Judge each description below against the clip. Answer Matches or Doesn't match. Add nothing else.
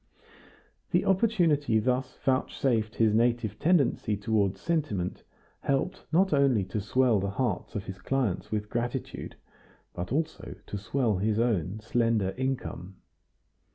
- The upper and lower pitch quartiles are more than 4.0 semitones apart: Matches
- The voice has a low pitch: Matches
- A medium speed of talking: Doesn't match